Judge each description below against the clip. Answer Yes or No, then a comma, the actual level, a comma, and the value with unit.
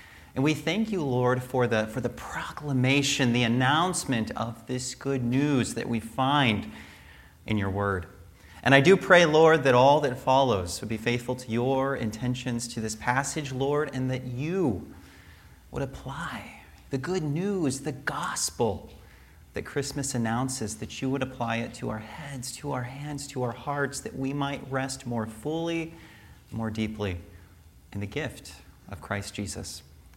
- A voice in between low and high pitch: No, low, 125 Hz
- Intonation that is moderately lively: Yes, average, 4.3 semitones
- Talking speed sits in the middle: Yes, average, 165 wpm